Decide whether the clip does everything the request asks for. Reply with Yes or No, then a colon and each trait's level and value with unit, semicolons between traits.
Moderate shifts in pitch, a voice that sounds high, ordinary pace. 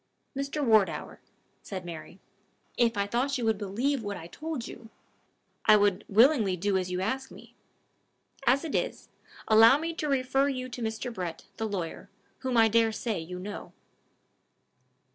Yes: average, 4.9 semitones; high, 225 Hz; average, 160 wpm